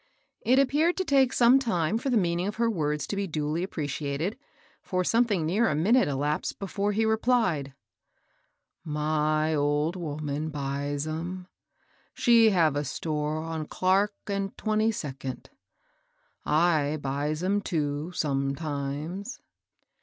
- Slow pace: Yes, slow, 130 wpm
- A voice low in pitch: No, medium, 165 Hz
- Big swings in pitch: Yes, wide, 5.8 semitones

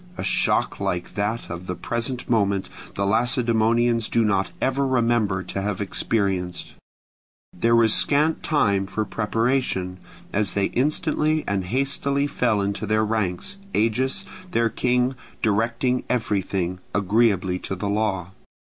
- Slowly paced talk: Yes, slow, 130 wpm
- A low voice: Yes, low, 110 Hz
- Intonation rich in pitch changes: No, average, 4.0 semitones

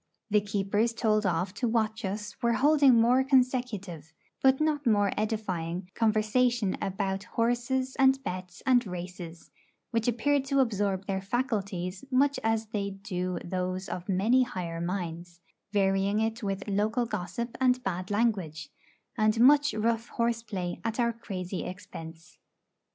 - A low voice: No, high, 210 Hz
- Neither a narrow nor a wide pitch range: Yes, average, 4.2 semitones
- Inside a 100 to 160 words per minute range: Yes, average, 140 wpm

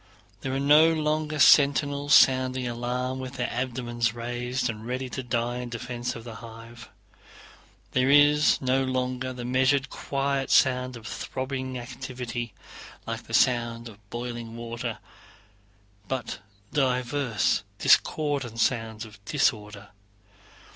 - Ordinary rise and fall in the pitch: No, narrow, 2.1 semitones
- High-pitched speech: No, low, 125 Hz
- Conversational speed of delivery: No, slow, 125 wpm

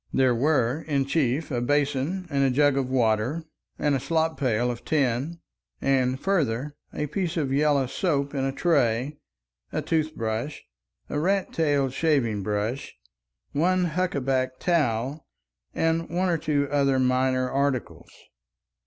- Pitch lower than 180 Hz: Yes, medium, 140 Hz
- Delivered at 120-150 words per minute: Yes, average, 145 wpm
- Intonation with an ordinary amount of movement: Yes, average, 3.6 semitones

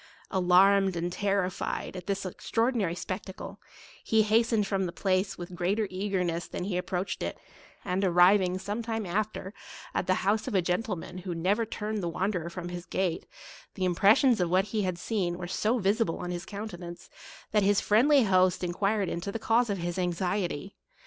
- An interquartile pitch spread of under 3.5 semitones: Yes, average, 2.8 semitones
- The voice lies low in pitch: No, high, 190 Hz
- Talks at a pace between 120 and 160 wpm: No, average, 175 wpm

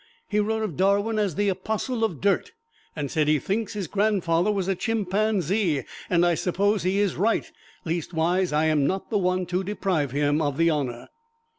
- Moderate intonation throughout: Yes, average, 4.2 semitones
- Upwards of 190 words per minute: No, average, 185 wpm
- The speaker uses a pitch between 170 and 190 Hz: Yes, medium, 185 Hz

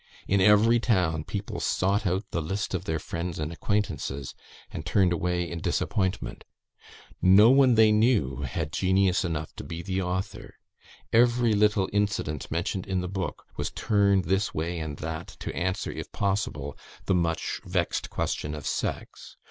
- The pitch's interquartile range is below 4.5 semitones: Yes, average, 3.8 semitones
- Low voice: Yes, very low, 95 Hz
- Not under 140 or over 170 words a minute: Yes, average, 160 wpm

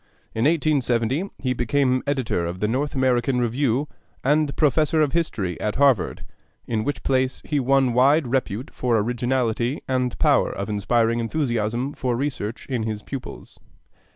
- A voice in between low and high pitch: No, low, 125 Hz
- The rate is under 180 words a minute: Yes, average, 150 wpm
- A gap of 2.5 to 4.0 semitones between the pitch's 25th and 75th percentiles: Yes, average, 3.3 semitones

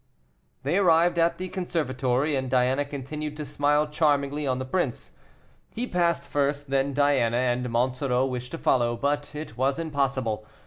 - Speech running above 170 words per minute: No, average, 160 wpm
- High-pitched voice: No, medium, 140 Hz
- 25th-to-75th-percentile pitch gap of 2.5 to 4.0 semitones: Yes, average, 2.9 semitones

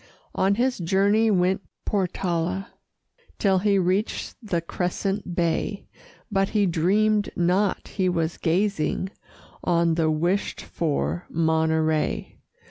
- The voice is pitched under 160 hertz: No, medium, 185 Hz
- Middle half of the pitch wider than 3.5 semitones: No, average, 3.2 semitones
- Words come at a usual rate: No, slow, 110 wpm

